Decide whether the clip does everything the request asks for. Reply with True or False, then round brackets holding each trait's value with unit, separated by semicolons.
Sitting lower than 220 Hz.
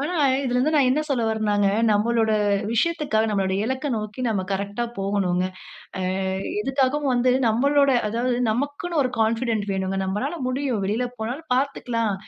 False (235 Hz)